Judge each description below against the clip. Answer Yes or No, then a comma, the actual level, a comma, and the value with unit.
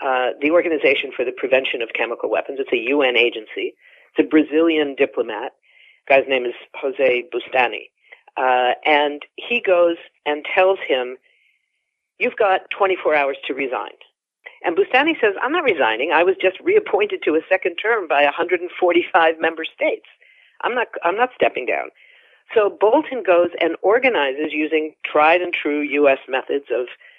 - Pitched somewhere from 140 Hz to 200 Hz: Yes, medium, 185 Hz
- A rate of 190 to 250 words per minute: No, average, 160 wpm